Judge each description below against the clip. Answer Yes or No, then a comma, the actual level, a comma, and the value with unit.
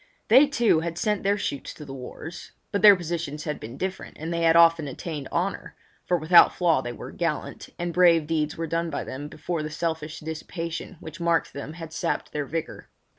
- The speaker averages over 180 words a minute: Yes, average, 200 wpm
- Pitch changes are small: Yes, narrow, 2.2 semitones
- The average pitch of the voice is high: No, medium, 165 Hz